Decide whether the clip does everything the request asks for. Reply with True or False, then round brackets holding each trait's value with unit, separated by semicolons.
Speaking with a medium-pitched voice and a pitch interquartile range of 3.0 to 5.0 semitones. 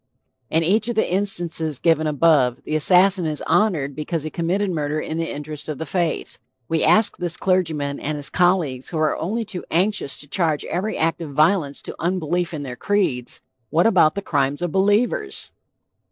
True (165 Hz; 3.7 semitones)